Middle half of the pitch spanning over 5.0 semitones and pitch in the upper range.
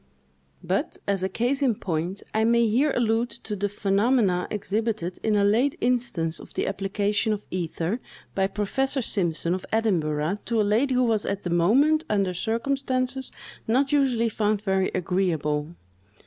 No: average, 4.3 semitones; high, 210 Hz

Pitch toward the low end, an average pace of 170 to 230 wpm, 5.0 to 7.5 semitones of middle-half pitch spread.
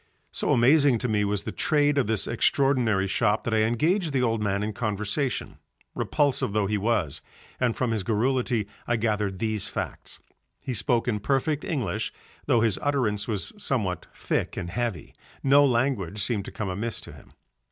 No: low, 115 Hz; average, 175 wpm; average, 4.0 semitones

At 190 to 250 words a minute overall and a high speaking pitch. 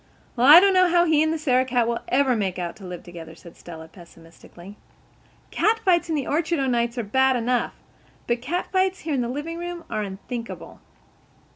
Yes: average, 195 wpm; very high, 255 Hz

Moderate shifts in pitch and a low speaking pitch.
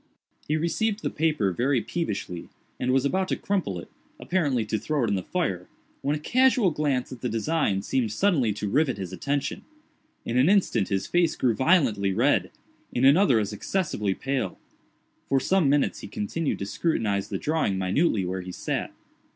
No: wide, 7.8 semitones; low, 130 Hz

